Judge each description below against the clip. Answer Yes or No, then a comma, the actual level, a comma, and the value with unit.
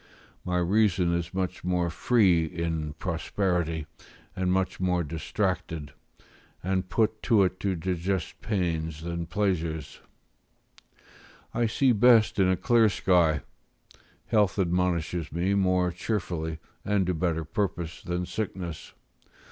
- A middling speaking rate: No, slow, 115 wpm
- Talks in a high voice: No, very low, 90 Hz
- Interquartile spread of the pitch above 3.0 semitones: No, average, 2.7 semitones